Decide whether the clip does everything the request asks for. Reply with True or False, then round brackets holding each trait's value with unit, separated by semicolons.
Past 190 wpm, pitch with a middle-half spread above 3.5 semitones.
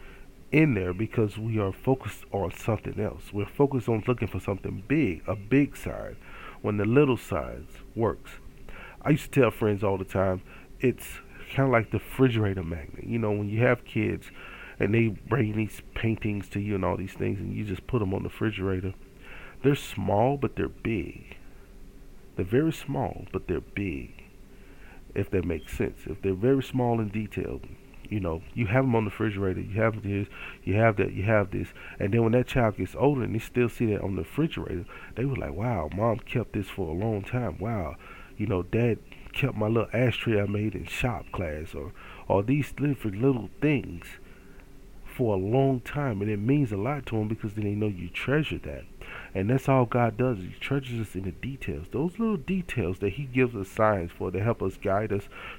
True (205 wpm; 4.4 semitones)